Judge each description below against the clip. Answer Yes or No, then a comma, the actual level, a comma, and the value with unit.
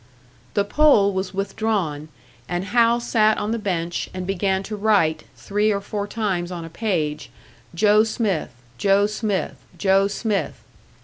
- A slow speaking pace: No, average, 145 wpm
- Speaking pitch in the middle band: No, high, 200 Hz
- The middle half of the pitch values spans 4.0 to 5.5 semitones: No, average, 2.8 semitones